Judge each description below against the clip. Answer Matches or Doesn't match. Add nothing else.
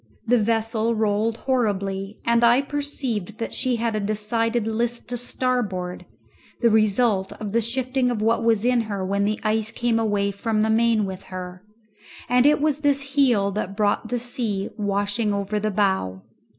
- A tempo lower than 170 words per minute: Doesn't match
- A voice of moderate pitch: Doesn't match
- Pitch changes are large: Doesn't match